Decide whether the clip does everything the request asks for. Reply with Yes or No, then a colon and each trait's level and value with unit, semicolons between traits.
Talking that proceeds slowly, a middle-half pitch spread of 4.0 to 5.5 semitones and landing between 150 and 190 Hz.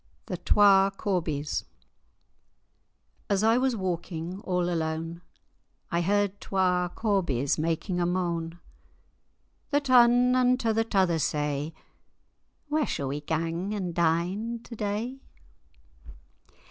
Yes: slow, 110 wpm; average, 4.7 semitones; medium, 185 Hz